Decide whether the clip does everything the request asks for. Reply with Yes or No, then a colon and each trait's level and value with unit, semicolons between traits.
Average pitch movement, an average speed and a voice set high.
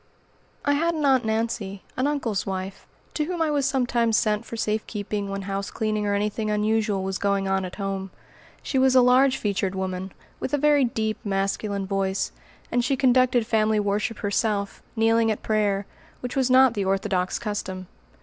Yes: average, 4.0 semitones; average, 180 wpm; high, 215 Hz